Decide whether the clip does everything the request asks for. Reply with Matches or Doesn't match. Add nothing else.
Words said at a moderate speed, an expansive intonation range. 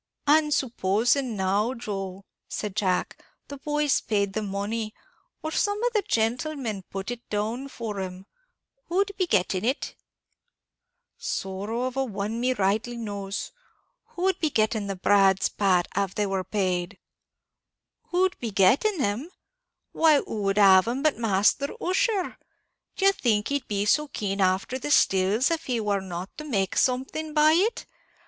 Matches